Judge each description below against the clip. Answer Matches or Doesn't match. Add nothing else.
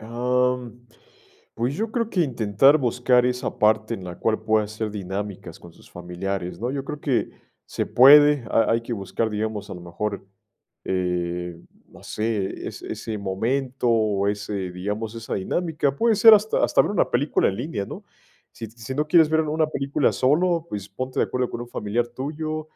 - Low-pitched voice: Matches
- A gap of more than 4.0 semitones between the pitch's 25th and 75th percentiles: Matches